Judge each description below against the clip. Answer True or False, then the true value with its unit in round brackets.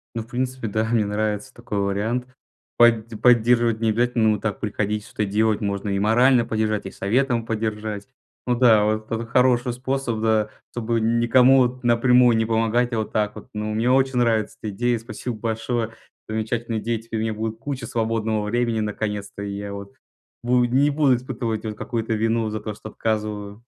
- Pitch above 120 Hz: False (110 Hz)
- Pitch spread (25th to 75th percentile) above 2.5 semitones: False (2.0 semitones)